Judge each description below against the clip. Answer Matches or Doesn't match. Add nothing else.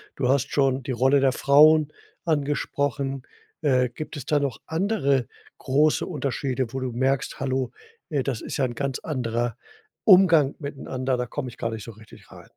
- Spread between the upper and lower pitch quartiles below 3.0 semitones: Matches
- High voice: Doesn't match